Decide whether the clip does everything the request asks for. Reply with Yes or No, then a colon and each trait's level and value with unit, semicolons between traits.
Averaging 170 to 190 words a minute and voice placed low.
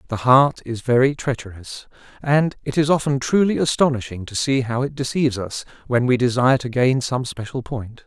Yes: average, 185 wpm; low, 130 Hz